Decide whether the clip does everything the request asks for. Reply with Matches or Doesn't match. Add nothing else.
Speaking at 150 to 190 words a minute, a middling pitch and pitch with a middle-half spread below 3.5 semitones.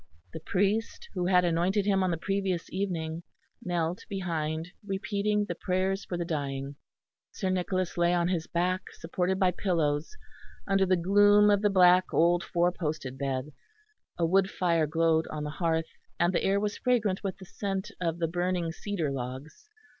Matches